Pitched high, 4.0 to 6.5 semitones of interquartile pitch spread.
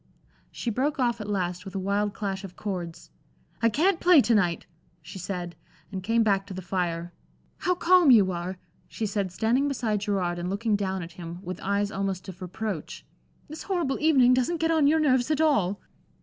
Yes: high, 205 Hz; wide, 5.6 semitones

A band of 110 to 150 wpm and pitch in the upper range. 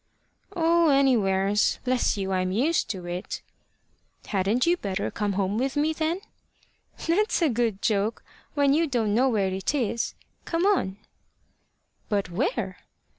Yes: average, 140 wpm; high, 235 Hz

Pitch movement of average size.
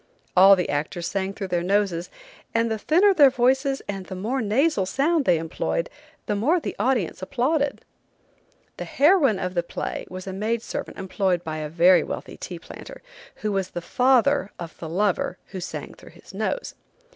No: wide, 6.6 semitones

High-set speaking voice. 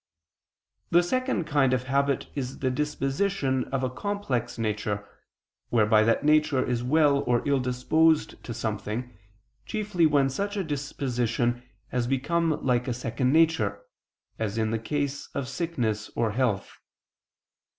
No: low, 130 Hz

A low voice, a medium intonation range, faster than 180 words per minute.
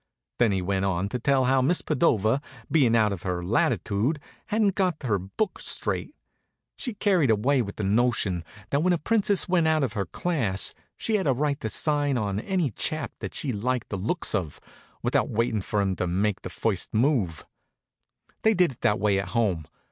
No: low, 120 Hz; wide, 7.4 semitones; average, 195 wpm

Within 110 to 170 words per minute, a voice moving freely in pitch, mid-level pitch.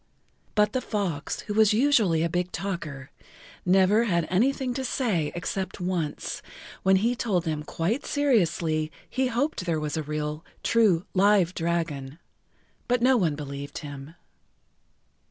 Yes: average, 145 wpm; wide, 6.0 semitones; medium, 180 Hz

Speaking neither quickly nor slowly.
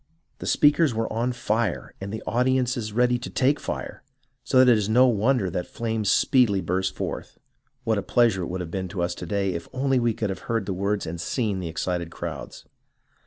No: fast, 210 wpm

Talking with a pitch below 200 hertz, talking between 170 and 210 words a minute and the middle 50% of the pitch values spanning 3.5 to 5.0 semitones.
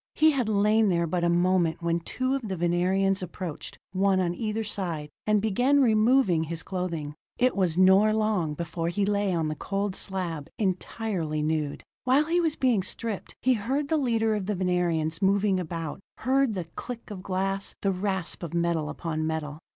Yes: high, 190 Hz; average, 180 wpm; average, 4.2 semitones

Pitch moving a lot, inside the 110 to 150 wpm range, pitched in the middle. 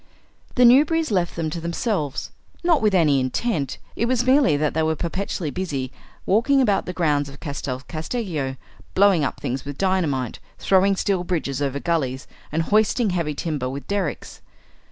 No: wide, 5.9 semitones; average, 165 wpm; medium, 170 Hz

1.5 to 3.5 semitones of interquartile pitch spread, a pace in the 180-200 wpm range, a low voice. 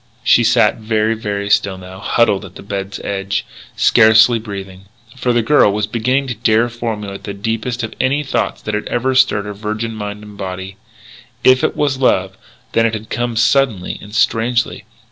Yes: average, 2.9 semitones; average, 185 wpm; low, 110 Hz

